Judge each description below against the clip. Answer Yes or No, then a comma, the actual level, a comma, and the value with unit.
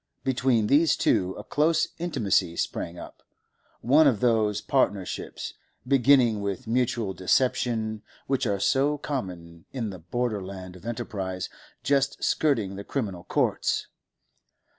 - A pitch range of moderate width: No, wide, 5.8 semitones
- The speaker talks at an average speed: No, slow, 125 wpm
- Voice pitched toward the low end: Yes, low, 115 Hz